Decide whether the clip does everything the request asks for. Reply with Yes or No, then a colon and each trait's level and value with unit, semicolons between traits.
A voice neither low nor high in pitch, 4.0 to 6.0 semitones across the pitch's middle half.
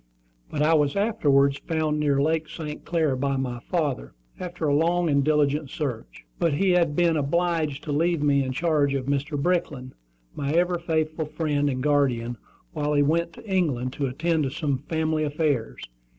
No: medium, 150 Hz; average, 2.8 semitones